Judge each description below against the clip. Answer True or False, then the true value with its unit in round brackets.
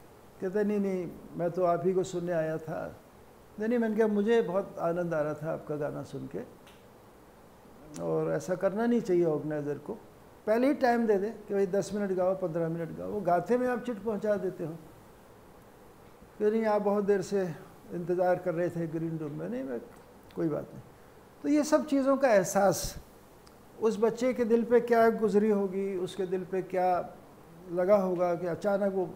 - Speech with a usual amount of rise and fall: True (3.7 semitones)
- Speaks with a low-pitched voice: False (190 Hz)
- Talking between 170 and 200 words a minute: True (190 wpm)